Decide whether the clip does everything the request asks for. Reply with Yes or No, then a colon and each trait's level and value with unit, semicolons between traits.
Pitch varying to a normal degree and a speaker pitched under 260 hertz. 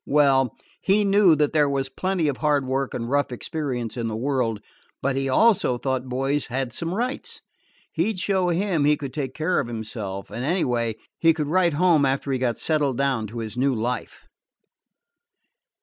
Yes: average, 4.5 semitones; medium, 140 Hz